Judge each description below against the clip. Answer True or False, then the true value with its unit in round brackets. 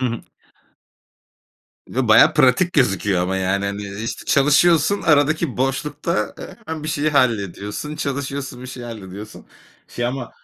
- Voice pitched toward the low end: True (130 Hz)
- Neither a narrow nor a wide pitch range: False (6.2 semitones)